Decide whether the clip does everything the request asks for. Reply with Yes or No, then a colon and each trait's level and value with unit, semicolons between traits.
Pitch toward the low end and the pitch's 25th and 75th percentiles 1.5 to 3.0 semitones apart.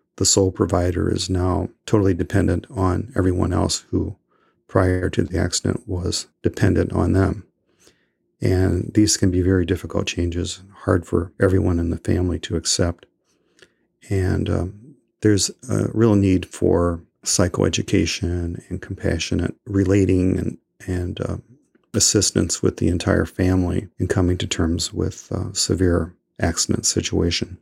Yes: very low, 95 Hz; narrow, 2.6 semitones